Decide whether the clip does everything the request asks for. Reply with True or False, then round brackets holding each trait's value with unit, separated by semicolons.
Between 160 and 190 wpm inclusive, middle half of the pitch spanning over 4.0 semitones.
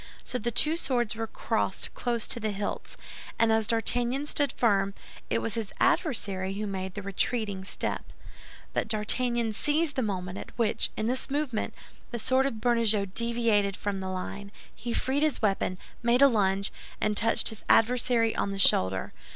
False (175 wpm; 3.4 semitones)